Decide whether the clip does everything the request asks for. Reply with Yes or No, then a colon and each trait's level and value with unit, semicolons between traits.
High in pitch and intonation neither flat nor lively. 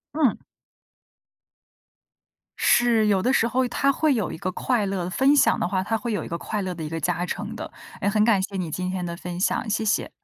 Yes: high, 200 Hz; average, 4.6 semitones